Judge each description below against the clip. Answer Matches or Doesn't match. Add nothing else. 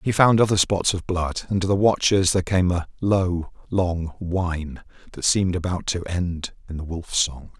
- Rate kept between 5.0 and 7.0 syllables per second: Doesn't match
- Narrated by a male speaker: Matches